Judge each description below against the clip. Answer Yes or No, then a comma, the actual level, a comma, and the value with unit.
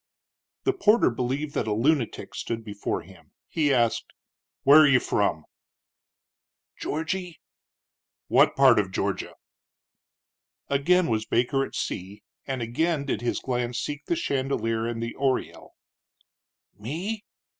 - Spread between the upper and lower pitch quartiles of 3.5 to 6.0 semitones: Yes, average, 5.1 semitones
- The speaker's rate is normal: No, slow, 125 wpm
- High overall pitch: No, low, 135 Hz